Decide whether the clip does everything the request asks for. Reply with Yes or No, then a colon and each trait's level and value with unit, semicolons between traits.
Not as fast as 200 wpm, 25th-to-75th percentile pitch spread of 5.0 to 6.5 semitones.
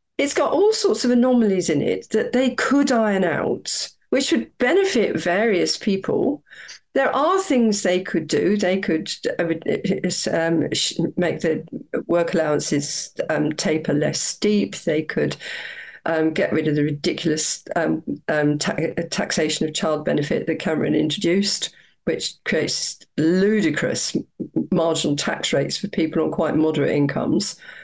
Yes: average, 140 wpm; wide, 5.6 semitones